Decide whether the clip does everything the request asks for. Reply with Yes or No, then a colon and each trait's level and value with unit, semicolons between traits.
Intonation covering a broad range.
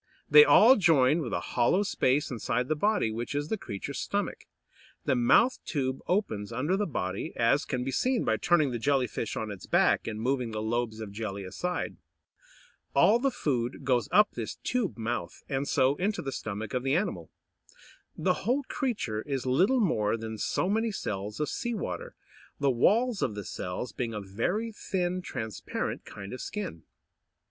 Yes: wide, 9.0 semitones